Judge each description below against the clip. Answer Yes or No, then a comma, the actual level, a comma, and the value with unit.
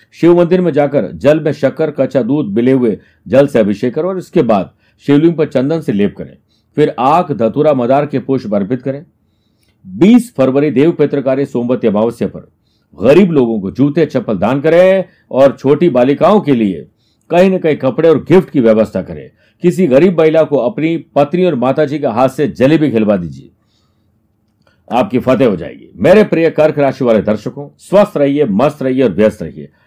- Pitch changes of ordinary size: No, wide, 5.9 semitones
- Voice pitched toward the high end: No, medium, 140 Hz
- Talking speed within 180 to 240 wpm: Yes, average, 185 wpm